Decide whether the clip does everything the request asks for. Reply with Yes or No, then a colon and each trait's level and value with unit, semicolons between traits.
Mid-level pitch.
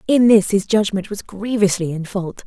No: high, 200 Hz